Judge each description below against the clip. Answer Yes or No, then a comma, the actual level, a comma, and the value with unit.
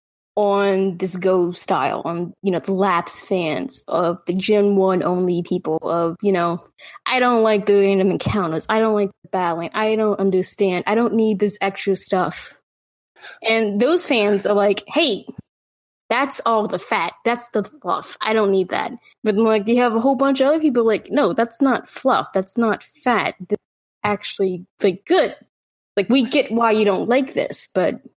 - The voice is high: Yes, high, 205 Hz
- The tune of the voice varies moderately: Yes, average, 3.3 semitones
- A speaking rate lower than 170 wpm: No, average, 185 wpm